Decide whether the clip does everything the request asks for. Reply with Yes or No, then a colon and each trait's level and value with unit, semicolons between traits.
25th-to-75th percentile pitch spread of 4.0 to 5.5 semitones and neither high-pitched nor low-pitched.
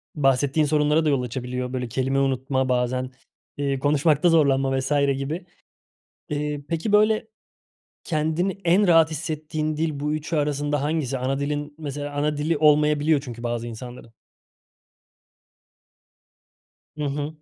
No: narrow, 2.6 semitones; medium, 145 Hz